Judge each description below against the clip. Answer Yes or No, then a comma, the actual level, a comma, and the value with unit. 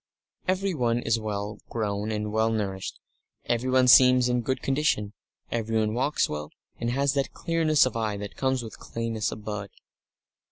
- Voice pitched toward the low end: Yes, low, 115 Hz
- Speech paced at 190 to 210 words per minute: No, average, 155 wpm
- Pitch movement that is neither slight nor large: Yes, average, 3.5 semitones